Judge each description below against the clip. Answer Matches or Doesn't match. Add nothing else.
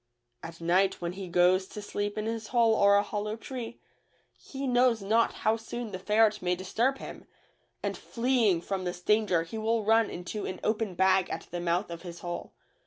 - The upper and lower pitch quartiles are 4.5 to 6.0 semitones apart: Doesn't match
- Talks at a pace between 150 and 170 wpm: Doesn't match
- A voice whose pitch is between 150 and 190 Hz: Doesn't match